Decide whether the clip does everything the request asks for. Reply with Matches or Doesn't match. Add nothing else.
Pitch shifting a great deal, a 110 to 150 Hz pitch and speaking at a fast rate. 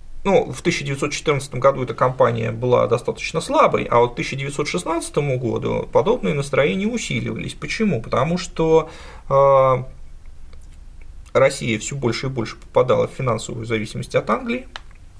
Doesn't match